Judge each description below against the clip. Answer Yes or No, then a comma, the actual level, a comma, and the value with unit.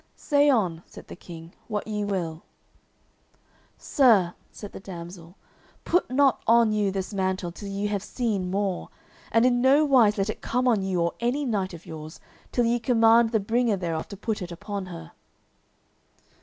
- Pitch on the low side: No, high, 205 Hz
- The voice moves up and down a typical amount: Yes, average, 4.4 semitones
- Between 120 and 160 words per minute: No, average, 175 wpm